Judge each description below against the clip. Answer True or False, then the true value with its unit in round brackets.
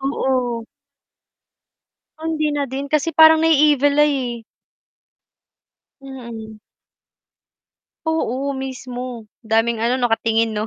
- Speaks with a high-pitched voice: True (260 Hz)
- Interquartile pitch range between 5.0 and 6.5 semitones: False (4.0 semitones)